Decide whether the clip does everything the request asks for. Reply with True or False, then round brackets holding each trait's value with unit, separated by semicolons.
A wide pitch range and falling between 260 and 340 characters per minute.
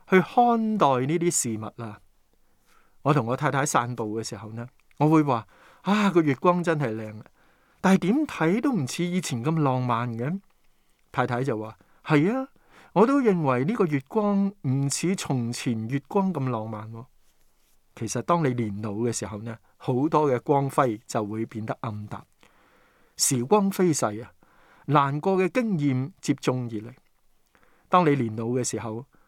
False (7.2 semitones; 220 characters per minute)